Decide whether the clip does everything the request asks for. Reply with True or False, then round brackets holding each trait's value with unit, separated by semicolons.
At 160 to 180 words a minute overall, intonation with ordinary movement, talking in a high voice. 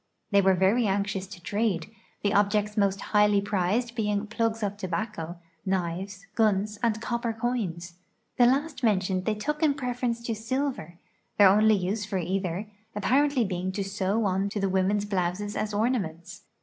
True (165 wpm; 3.0 semitones; 205 Hz)